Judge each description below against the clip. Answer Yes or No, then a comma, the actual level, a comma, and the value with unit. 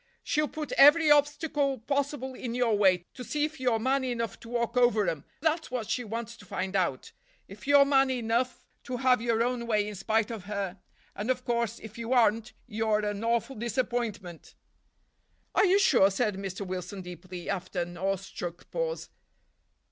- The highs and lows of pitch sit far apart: No, average, 4.5 semitones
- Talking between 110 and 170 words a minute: No, average, 180 wpm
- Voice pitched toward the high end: Yes, high, 230 Hz